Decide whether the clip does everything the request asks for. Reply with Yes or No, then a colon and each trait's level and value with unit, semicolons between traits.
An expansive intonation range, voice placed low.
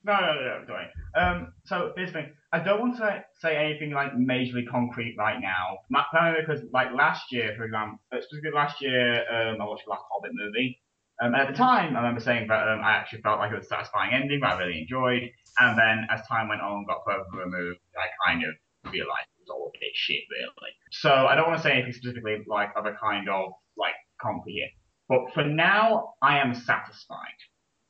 Yes: wide, 5.9 semitones; low, 120 Hz